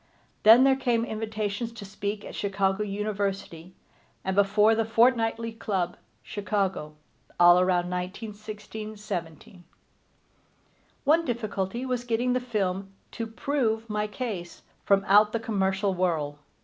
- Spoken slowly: Yes, slow, 125 wpm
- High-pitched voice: Yes, high, 210 Hz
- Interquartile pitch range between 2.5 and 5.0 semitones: Yes, average, 2.8 semitones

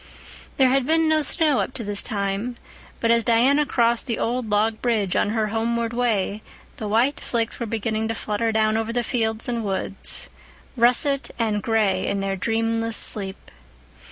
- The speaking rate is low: No, average, 175 wpm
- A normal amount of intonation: No, narrow, 2.1 semitones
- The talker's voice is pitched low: No, high, 225 Hz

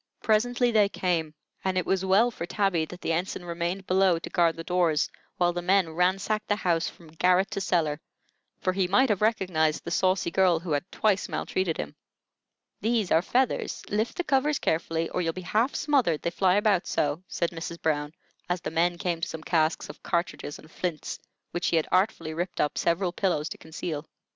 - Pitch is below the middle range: No, medium, 180 Hz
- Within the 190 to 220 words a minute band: Yes, average, 200 wpm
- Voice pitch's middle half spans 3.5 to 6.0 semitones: No, average, 3.0 semitones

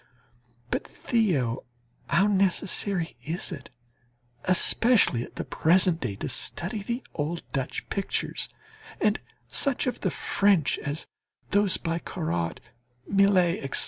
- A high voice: No, medium, 180 Hz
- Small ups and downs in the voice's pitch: No, average, 4.4 semitones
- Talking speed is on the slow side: Yes, slow, 120 wpm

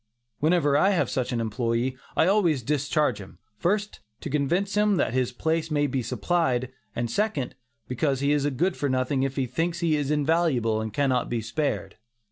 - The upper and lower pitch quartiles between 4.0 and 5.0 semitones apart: Yes, average, 4.5 semitones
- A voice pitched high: No, medium, 140 Hz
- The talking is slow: No, average, 185 wpm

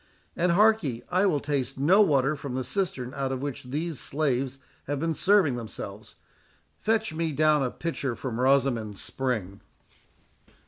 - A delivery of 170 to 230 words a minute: No, average, 150 wpm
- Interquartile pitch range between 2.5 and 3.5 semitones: No, average, 4.5 semitones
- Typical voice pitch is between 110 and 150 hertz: Yes, medium, 140 Hz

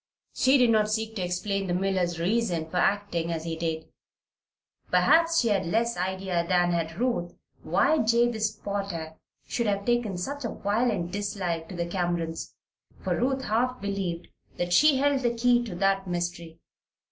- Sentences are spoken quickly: No, average, 165 wpm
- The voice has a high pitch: Yes, high, 195 Hz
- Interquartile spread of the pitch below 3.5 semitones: No, average, 5.1 semitones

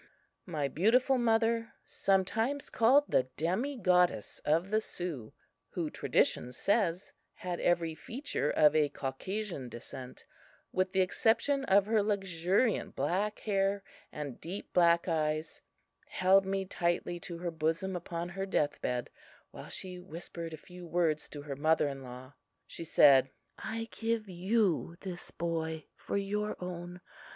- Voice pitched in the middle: Yes, medium, 180 Hz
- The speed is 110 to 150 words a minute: Yes, average, 140 wpm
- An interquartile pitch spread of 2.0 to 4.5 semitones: Yes, average, 4.1 semitones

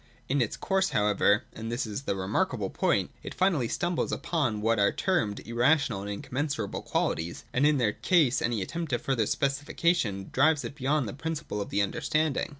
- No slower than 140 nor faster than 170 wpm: No, average, 180 wpm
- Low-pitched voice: Yes, low, 125 Hz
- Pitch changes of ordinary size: No, wide, 6.5 semitones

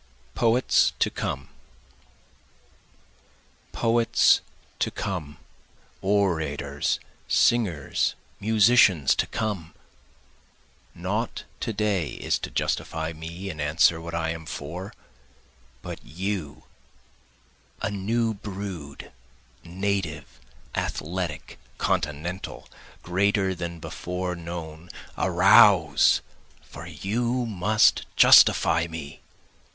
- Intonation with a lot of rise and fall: No, average, 4.0 semitones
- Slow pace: Yes, slow, 85 wpm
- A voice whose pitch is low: Yes, very low, 90 Hz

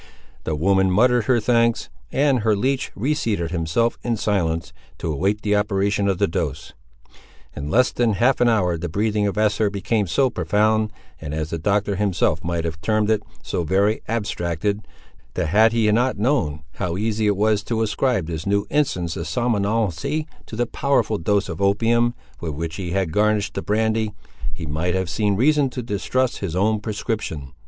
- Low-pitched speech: Yes, low, 105 Hz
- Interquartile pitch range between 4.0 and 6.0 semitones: Yes, average, 4.3 semitones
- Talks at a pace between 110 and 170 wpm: No, average, 180 wpm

